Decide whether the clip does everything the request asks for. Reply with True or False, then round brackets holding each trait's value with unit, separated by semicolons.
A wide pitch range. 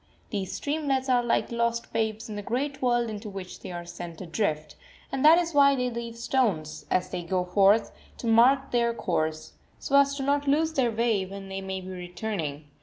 True (5.9 semitones)